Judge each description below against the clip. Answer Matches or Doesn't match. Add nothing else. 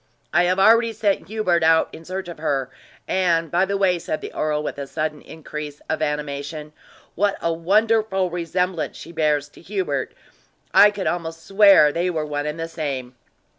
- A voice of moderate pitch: Matches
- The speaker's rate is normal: Matches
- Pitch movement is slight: Doesn't match